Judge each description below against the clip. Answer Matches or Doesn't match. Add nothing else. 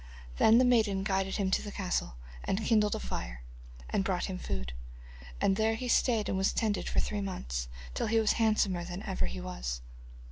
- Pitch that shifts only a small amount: Doesn't match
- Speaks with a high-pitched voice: Matches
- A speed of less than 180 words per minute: Doesn't match